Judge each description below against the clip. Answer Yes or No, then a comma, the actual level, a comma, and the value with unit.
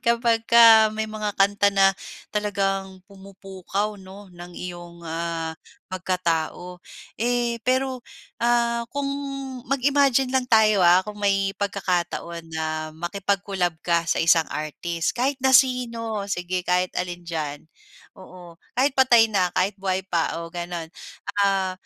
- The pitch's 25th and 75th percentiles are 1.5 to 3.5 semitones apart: No, average, 4.5 semitones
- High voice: Yes, high, 195 Hz